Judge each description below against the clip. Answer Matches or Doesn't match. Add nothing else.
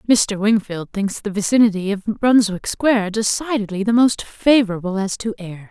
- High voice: Matches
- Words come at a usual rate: Matches